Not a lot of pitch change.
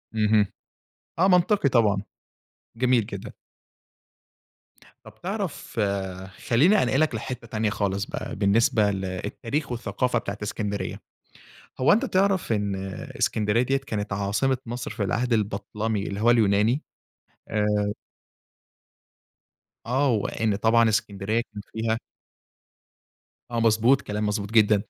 No: average, 3.4 semitones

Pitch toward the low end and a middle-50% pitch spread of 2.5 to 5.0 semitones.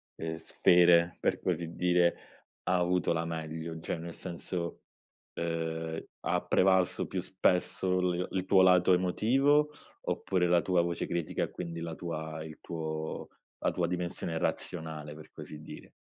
No: very low, 85 Hz; narrow, 1.9 semitones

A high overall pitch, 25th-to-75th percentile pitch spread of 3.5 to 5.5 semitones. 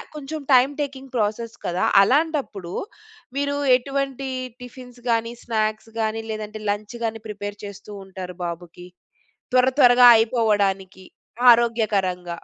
Yes: high, 225 Hz; average, 3.8 semitones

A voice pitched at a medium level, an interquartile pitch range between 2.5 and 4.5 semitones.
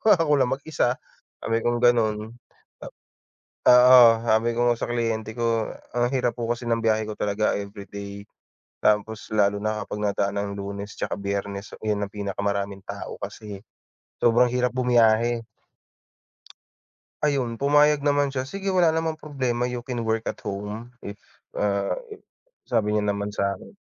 No: low, 115 Hz; average, 3.3 semitones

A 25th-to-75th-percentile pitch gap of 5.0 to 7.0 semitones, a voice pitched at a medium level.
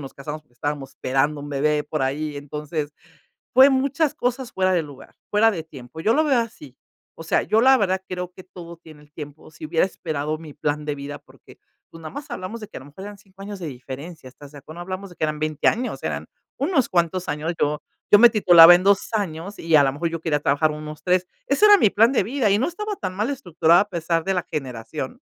Yes: wide, 5.5 semitones; medium, 165 Hz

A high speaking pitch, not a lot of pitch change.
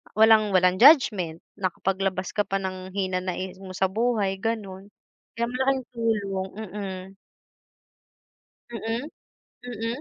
No: high, 195 Hz; average, 3.2 semitones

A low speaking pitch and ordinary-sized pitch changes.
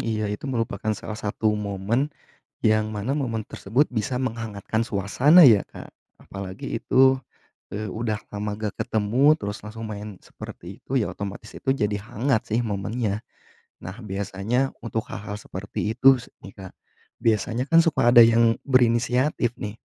Yes: low, 110 Hz; average, 3.1 semitones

